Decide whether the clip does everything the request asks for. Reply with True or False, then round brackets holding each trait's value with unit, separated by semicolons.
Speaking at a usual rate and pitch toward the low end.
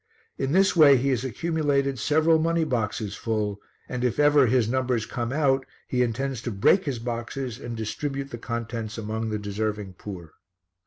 True (170 wpm; 125 Hz)